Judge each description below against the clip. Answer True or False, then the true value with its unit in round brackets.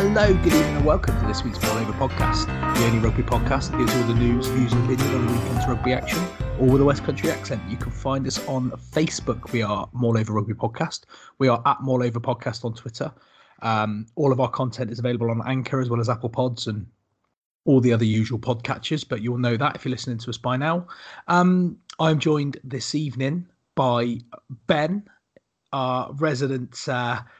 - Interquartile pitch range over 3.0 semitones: False (2.5 semitones)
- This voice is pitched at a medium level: False (125 Hz)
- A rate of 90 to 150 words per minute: False (200 wpm)